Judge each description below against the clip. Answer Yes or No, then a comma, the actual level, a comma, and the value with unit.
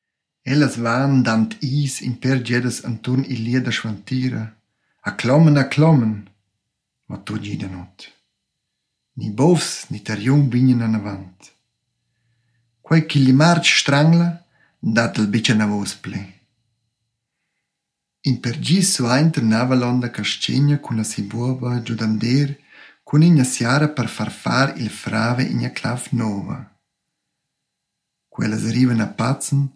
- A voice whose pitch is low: Yes, low, 125 Hz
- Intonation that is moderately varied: Yes, average, 4.0 semitones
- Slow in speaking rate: Yes, slow, 125 wpm